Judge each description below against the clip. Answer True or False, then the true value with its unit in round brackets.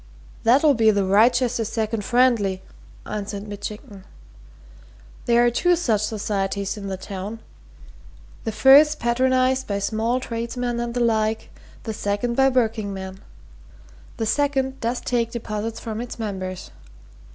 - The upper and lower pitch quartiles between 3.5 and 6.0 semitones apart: False (3.1 semitones)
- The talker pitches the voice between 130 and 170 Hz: False (225 Hz)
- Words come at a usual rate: False (130 wpm)